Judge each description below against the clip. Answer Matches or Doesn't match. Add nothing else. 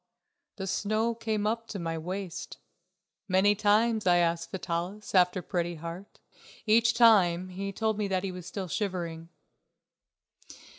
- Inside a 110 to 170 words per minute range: Matches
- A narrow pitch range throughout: Doesn't match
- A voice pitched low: Doesn't match